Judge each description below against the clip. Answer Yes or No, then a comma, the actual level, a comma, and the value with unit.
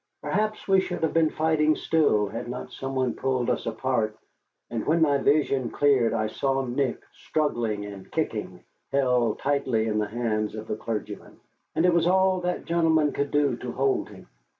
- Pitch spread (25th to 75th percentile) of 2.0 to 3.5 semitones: No, average, 5.3 semitones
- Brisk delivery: No, average, 180 wpm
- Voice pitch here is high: No, low, 135 Hz